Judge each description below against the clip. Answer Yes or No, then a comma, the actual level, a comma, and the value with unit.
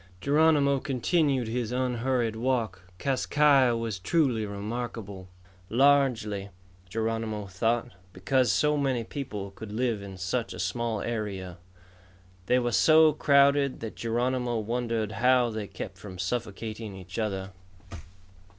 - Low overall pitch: Yes, low, 115 Hz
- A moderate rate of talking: No, slow, 125 wpm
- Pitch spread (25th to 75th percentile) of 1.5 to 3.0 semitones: No, average, 3.8 semitones